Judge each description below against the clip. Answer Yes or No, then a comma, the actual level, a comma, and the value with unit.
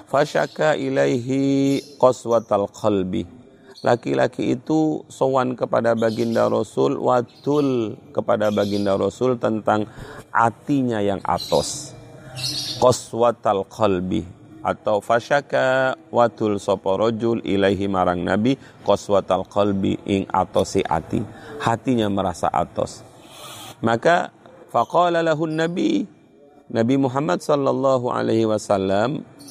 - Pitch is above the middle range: No, low, 120 Hz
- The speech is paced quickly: No, average, 90 wpm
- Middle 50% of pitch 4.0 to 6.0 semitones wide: Yes, average, 5.0 semitones